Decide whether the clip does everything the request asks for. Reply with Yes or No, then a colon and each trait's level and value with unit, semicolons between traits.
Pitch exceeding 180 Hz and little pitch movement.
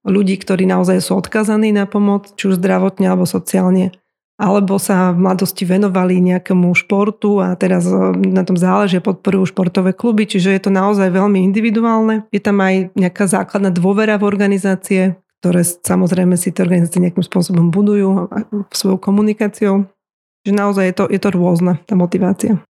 Yes: high, 190 Hz; narrow, 1.6 semitones